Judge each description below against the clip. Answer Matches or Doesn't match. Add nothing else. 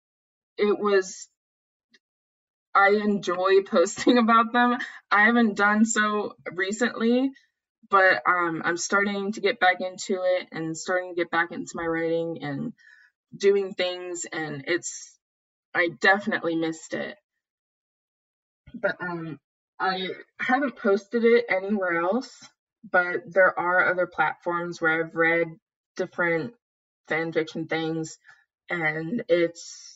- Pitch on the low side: Doesn't match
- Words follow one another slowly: Matches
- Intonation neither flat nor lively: Matches